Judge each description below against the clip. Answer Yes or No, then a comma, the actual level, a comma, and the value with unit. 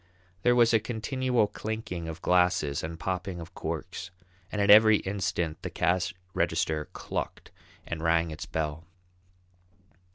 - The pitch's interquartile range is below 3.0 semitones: No, average, 4.6 semitones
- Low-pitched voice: Yes, very low, 90 Hz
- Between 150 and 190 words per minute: No, slow, 135 wpm